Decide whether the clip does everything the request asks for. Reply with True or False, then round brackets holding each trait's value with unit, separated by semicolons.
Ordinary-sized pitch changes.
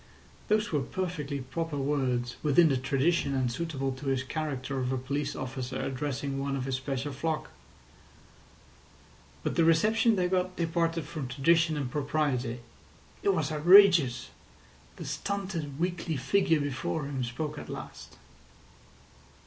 True (3.9 semitones)